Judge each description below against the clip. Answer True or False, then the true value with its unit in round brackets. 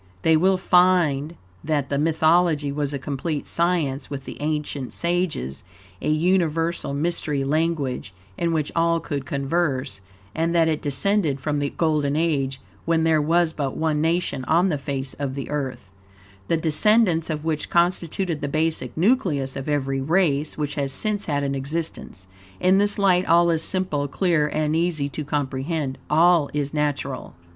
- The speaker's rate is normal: True (160 wpm)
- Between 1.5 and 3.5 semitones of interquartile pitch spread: True (3.2 semitones)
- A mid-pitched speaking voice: True (155 Hz)